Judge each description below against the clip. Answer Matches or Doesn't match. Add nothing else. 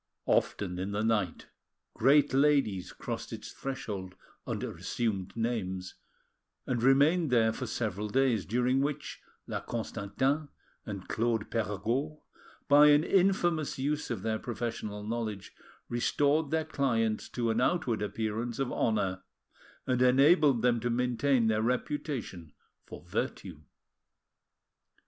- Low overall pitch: Matches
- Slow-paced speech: Matches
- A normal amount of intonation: Matches